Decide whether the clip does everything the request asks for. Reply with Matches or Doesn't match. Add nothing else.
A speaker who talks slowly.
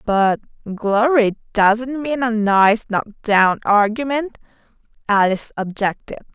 Matches